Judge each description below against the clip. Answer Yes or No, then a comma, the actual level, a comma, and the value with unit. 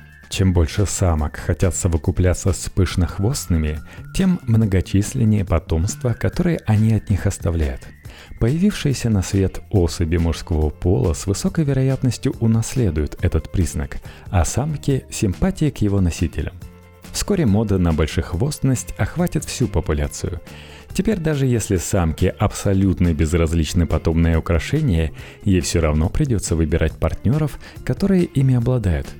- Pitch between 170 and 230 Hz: No, very low, 95 Hz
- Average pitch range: No, wide, 6.0 semitones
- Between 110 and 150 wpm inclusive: Yes, average, 115 wpm